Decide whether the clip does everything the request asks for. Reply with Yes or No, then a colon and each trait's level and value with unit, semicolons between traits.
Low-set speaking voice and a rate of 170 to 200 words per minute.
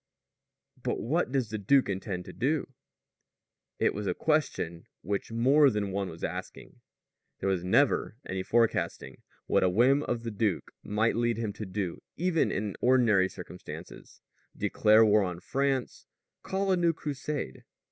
No: low, 110 Hz; average, 155 wpm